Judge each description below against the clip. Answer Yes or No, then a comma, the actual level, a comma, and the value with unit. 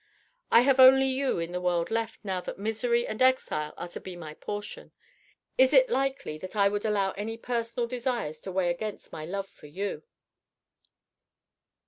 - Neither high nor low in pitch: No, high, 210 Hz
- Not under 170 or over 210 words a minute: Yes, average, 175 wpm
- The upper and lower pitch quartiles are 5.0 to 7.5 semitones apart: Yes, wide, 5.6 semitones